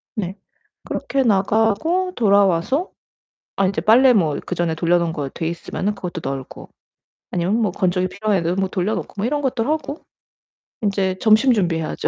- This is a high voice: Yes, high, 195 Hz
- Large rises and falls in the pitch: No, average, 4.3 semitones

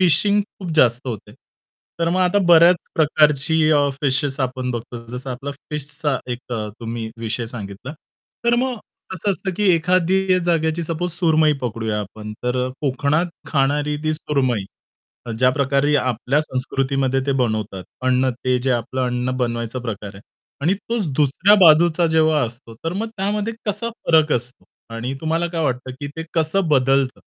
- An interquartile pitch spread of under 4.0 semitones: No, average, 4.9 semitones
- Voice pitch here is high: No, medium, 140 Hz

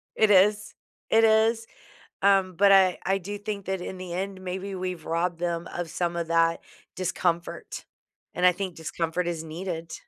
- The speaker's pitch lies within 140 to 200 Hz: Yes, medium, 185 Hz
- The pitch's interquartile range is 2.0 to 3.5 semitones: Yes, narrow, 2.4 semitones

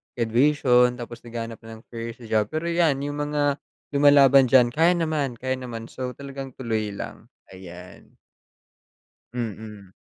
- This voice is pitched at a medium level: No, low, 125 Hz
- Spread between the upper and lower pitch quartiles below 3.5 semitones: No, average, 3.8 semitones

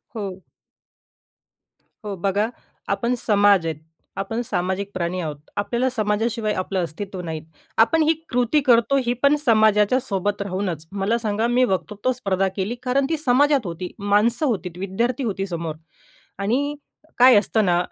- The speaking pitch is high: Yes, high, 205 Hz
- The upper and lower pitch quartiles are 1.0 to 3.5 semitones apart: No, average, 4.2 semitones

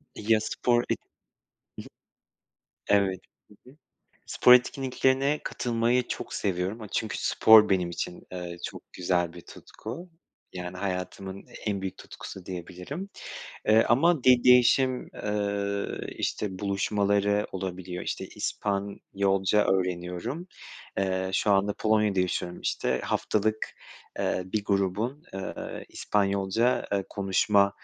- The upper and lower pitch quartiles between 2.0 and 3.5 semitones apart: Yes, average, 3.0 semitones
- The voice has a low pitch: Yes, low, 100 Hz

